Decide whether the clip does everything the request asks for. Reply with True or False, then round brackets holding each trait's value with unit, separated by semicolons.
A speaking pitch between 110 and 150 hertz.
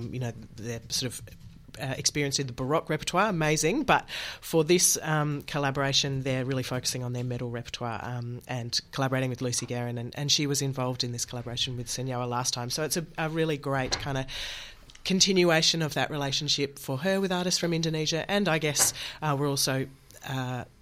True (135 Hz)